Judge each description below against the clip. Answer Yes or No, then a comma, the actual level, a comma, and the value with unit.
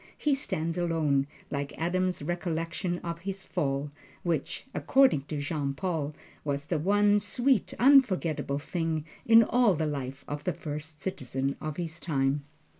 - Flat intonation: No, average, 4.2 semitones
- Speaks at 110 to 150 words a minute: Yes, average, 145 wpm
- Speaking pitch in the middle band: Yes, medium, 165 Hz